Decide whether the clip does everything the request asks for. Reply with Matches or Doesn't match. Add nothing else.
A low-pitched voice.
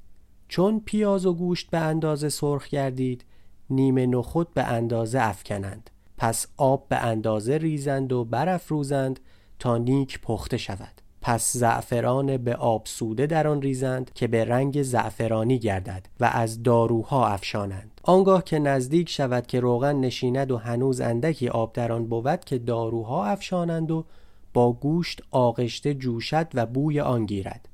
Matches